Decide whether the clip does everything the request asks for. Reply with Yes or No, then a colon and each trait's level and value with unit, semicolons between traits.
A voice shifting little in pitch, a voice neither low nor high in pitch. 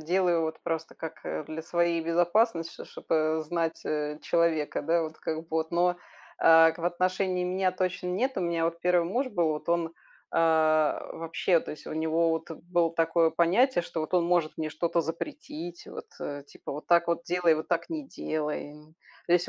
Yes: narrow, 1.8 semitones; medium, 170 Hz